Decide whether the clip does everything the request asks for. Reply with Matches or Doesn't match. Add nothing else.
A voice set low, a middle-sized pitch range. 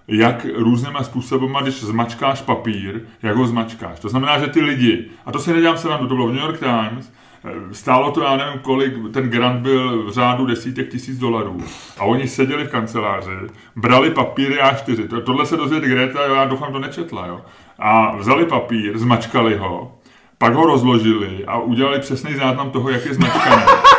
Matches